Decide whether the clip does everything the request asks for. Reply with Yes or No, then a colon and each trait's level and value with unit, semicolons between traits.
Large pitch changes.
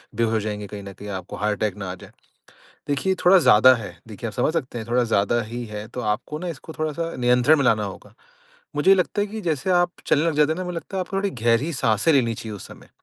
Yes: wide, 7.5 semitones